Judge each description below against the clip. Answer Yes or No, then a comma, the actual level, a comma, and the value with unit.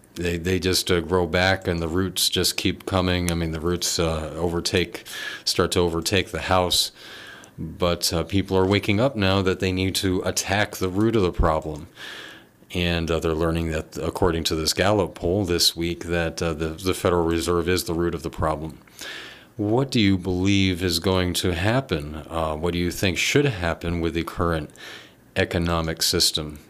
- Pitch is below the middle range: Yes, very low, 85 Hz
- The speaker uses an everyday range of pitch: No, narrow, 2.1 semitones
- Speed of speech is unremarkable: Yes, average, 185 wpm